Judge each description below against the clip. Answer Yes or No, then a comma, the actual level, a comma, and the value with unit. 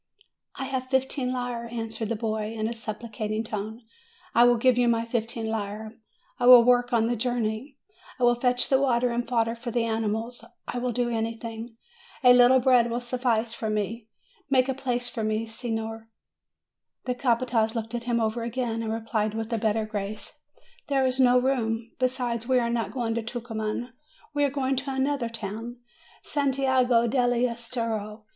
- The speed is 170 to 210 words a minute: Yes, average, 180 wpm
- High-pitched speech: Yes, high, 235 Hz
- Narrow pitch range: Yes, narrow, 1.9 semitones